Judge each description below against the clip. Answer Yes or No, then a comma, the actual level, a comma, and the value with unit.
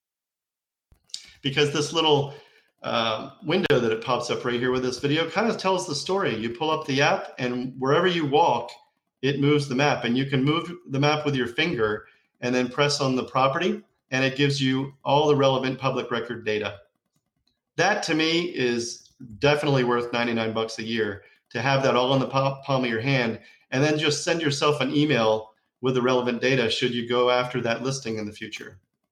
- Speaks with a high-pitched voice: No, low, 135 Hz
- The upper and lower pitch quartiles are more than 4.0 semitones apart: No, average, 3.3 semitones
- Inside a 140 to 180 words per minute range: No, average, 200 wpm